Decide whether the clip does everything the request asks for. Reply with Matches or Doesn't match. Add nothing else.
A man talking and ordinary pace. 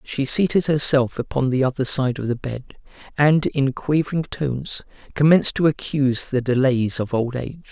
Matches